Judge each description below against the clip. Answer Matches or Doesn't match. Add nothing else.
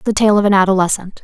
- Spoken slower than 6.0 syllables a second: Doesn't match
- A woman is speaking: Matches